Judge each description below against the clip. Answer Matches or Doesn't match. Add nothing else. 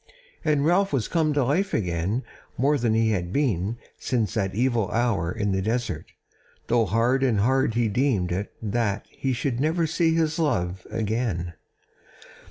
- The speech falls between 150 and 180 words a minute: Matches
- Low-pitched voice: Matches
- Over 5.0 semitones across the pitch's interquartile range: Matches